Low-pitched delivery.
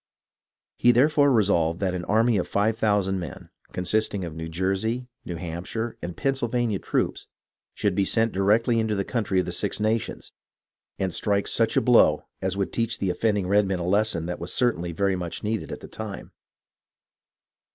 Yes: low, 100 Hz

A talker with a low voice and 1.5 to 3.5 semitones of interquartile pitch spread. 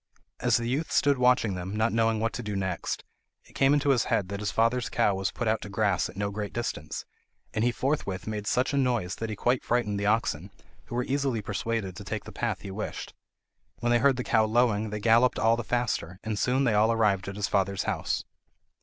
Yes: low, 110 Hz; average, 3.1 semitones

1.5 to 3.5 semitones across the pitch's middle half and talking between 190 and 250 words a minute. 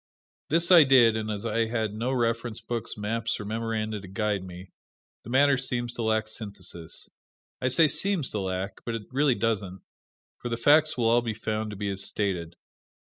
Yes: average, 2.8 semitones; average, 195 wpm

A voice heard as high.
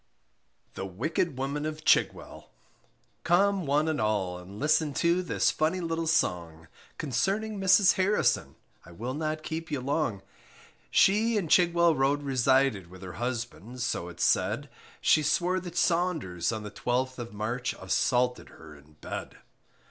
No: medium, 140 Hz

